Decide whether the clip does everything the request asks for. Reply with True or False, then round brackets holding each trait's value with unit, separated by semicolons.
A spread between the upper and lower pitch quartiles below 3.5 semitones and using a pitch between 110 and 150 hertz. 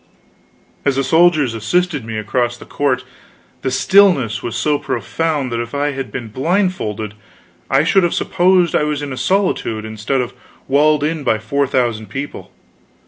False (5.2 semitones; 135 Hz)